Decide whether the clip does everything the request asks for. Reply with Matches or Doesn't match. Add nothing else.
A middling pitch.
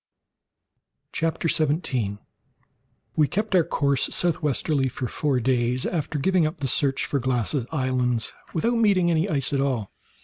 Matches